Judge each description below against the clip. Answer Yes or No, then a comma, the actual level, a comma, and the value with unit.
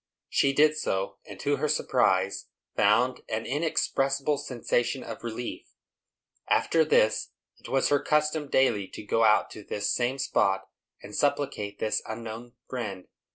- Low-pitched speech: Yes, low, 120 Hz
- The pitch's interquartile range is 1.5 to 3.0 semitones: No, average, 4.6 semitones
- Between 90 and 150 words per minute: Yes, average, 145 wpm